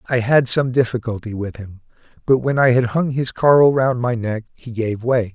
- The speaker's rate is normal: No, fast, 215 wpm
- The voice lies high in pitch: No, low, 120 Hz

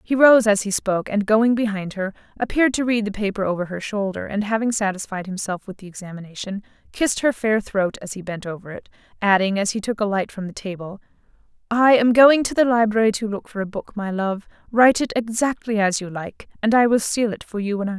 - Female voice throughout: Yes, female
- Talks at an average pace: No, fast, 235 wpm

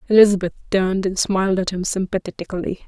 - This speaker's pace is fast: No, average, 145 wpm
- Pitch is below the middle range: No, high, 190 Hz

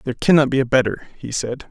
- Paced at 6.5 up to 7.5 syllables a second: Yes, 6.6 syllables/s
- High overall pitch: No, low, 130 Hz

